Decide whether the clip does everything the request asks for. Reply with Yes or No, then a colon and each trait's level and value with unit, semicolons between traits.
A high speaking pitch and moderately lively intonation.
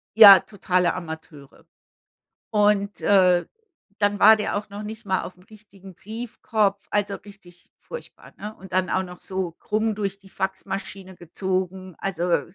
No: high, 195 Hz; narrow, 2.1 semitones